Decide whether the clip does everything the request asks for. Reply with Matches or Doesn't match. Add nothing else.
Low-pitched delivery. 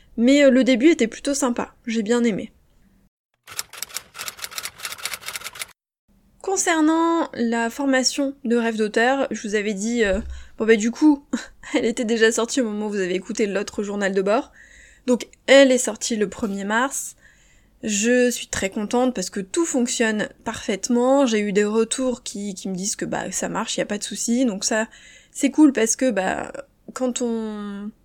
Doesn't match